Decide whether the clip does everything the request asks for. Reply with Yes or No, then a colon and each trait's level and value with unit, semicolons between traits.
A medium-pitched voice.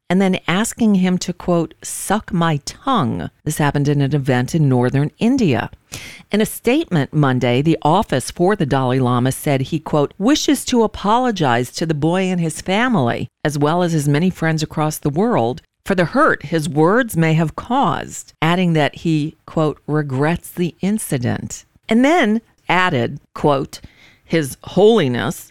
Yes: medium, 160 Hz